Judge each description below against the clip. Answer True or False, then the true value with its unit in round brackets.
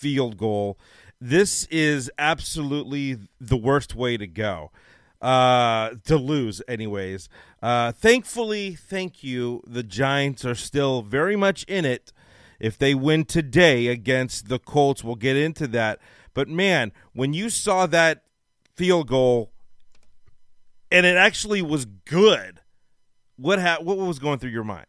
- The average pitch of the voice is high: False (135 Hz)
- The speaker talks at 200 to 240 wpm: False (140 wpm)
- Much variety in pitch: True (5.7 semitones)